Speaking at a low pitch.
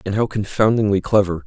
Yes: low, 100 Hz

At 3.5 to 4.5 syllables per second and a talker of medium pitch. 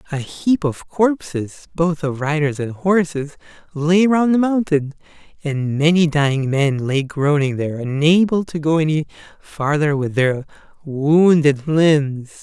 Yes: 4.0 syllables/s; medium, 155 Hz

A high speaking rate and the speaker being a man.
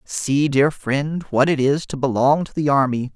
Yes: fast, 210 wpm; male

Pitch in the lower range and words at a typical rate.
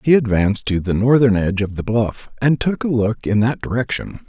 No: low, 115 Hz; fast, 225 wpm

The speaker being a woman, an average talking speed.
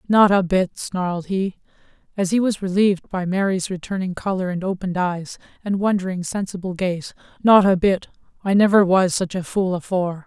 Yes: female; average, 175 wpm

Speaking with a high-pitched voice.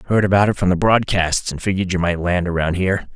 No: very low, 95 Hz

